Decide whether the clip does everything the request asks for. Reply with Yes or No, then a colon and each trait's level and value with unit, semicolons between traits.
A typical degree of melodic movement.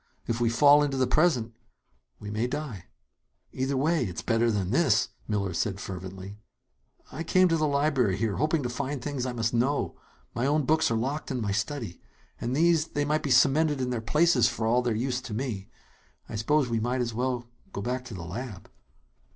Yes: average, 4.5 semitones